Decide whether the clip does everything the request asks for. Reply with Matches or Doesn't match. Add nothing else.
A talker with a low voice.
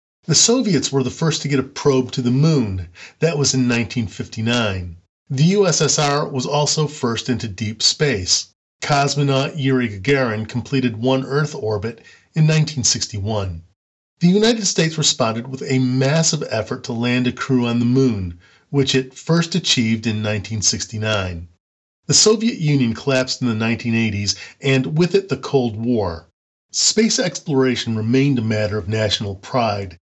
Matches